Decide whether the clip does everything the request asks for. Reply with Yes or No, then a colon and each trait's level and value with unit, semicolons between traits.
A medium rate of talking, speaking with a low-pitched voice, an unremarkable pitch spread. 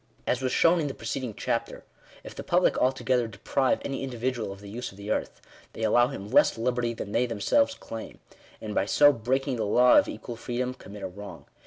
No: fast, 210 wpm; low, 120 Hz; average, 3.4 semitones